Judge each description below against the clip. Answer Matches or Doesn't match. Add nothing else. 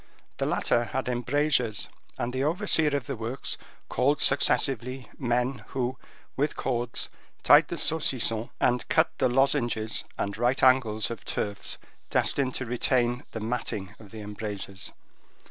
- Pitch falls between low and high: Doesn't match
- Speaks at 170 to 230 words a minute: Doesn't match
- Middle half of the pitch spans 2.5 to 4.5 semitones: Matches